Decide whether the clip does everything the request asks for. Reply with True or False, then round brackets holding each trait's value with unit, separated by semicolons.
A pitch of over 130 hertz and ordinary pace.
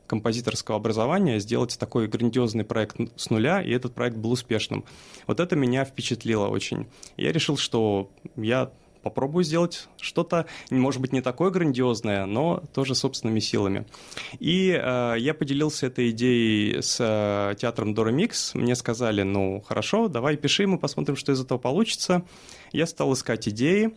False (125 Hz; 150 wpm)